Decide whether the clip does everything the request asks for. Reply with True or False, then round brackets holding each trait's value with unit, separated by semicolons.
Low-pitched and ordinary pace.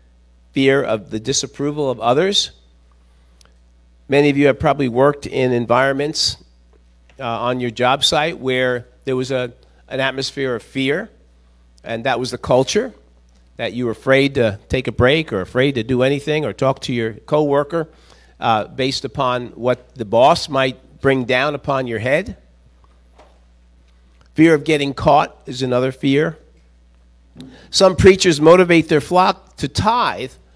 True (125 Hz; 150 wpm)